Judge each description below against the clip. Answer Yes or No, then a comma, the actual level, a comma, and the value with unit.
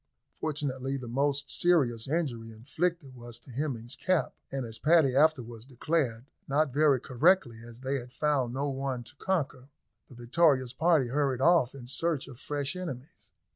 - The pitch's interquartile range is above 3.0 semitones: Yes, average, 3.8 semitones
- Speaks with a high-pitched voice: No, low, 135 Hz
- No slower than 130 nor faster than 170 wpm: Yes, average, 160 wpm